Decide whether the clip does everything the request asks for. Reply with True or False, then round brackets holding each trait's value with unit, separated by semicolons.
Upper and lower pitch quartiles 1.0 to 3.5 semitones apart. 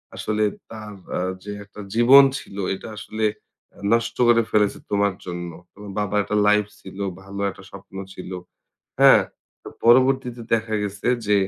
True (2.7 semitones)